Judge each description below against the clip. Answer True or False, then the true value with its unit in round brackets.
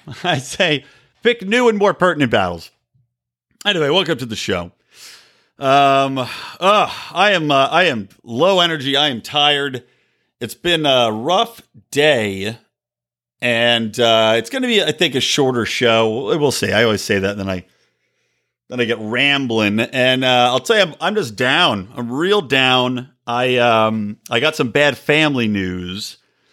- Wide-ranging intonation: False (4.5 semitones)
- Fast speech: False (165 wpm)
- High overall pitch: False (125 Hz)